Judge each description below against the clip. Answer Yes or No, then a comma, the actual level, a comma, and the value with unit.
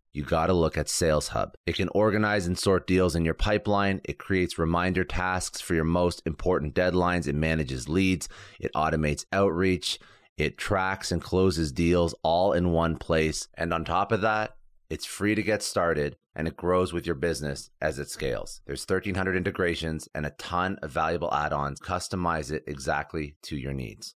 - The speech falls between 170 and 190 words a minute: Yes, average, 180 wpm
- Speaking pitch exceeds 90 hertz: No, very low, 85 Hz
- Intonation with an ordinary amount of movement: Yes, average, 3.1 semitones